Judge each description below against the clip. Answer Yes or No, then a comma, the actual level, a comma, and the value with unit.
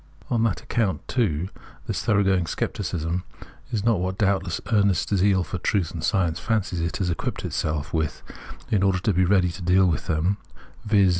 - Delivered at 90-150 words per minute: No, average, 200 wpm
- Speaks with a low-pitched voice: Yes, very low, 95 Hz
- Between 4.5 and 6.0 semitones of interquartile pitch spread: No, average, 2.8 semitones